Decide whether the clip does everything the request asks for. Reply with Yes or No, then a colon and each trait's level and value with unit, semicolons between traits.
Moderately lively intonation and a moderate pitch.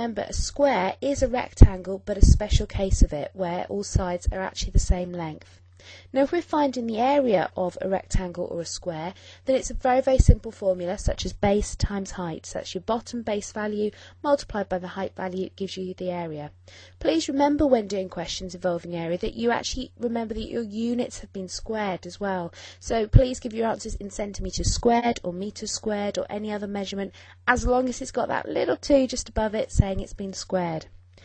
No: average, 4.8 semitones; high, 200 Hz